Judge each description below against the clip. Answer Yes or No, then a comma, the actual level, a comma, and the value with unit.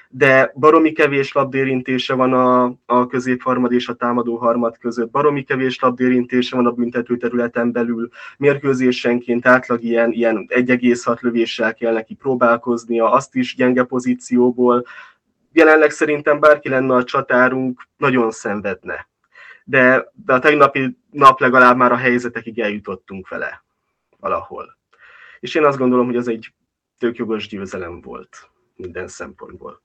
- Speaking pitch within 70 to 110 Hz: No, low, 125 Hz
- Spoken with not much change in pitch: Yes, narrow, 1.7 semitones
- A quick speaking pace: No, average, 135 wpm